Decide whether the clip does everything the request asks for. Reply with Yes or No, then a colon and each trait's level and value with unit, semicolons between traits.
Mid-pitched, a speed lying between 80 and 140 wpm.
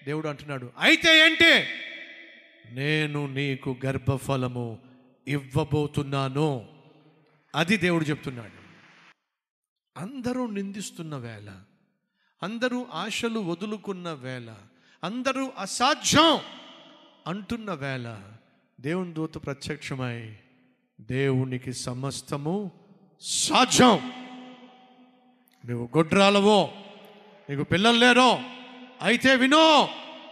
No: medium, 165 Hz; slow, 70 wpm